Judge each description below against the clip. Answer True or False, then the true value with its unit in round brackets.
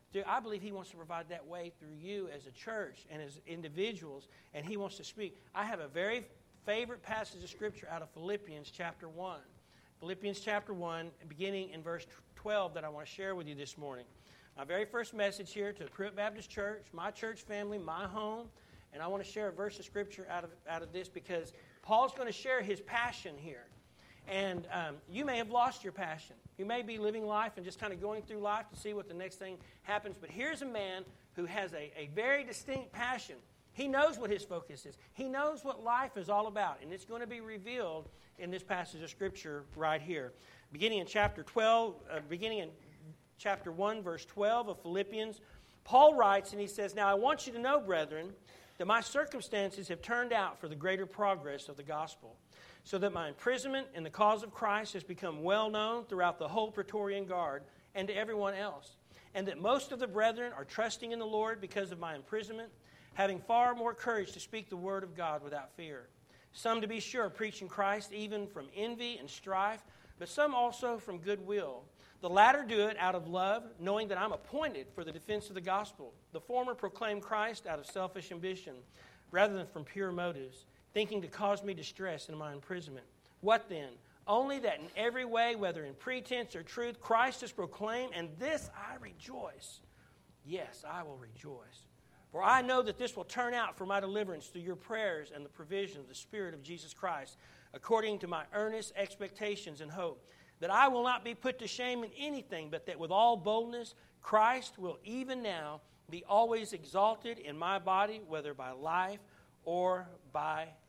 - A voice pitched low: False (200 Hz)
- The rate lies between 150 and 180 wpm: False (205 wpm)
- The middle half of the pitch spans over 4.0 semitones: True (4.5 semitones)